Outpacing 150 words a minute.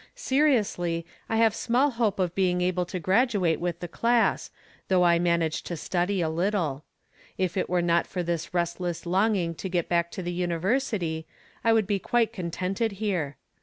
Yes: average, 175 wpm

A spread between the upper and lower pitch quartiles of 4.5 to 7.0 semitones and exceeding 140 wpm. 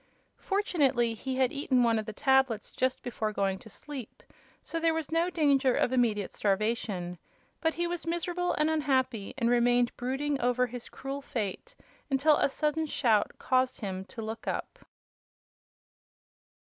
Yes: average, 4.8 semitones; average, 155 wpm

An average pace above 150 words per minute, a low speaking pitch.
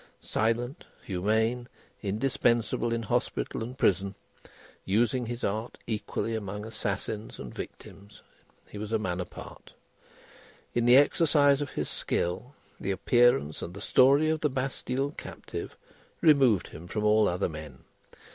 No: slow, 135 wpm; low, 110 Hz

